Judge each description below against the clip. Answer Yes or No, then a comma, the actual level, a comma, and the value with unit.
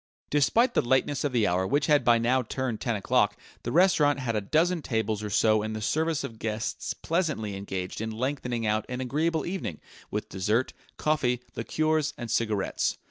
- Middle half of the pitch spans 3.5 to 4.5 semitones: No, average, 5.3 semitones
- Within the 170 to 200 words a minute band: Yes, average, 185 wpm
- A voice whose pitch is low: Yes, low, 125 Hz